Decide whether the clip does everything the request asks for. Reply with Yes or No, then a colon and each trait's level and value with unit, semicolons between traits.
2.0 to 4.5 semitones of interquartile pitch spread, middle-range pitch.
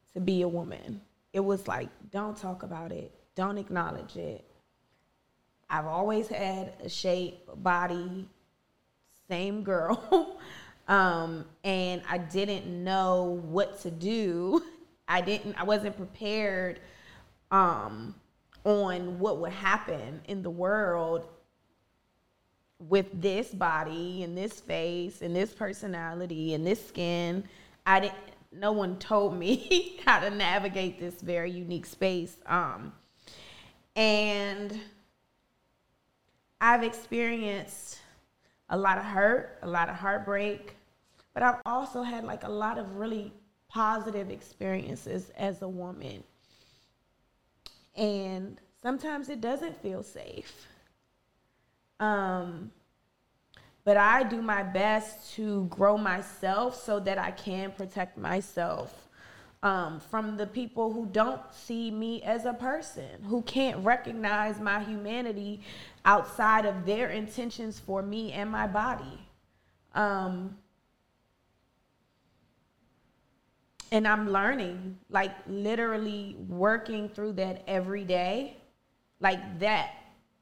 No: average, 2.8 semitones; high, 200 Hz